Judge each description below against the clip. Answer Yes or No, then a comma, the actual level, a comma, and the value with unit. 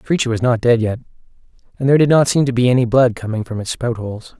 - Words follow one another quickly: Yes, fast, 275 wpm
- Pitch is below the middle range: Yes, low, 120 Hz